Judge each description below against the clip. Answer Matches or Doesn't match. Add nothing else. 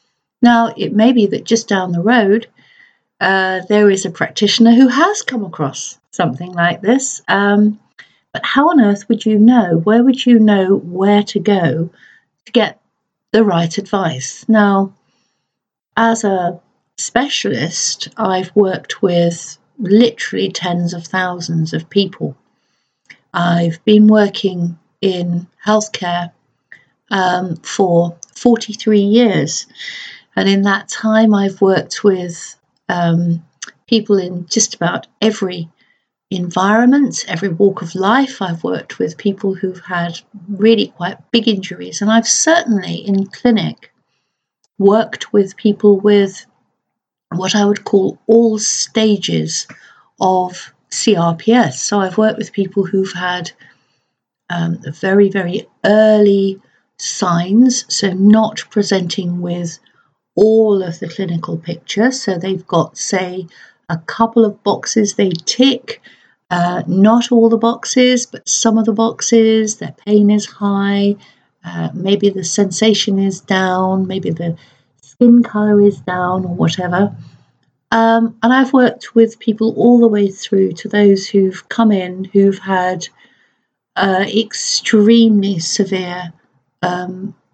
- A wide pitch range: Doesn't match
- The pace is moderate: Doesn't match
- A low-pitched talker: Doesn't match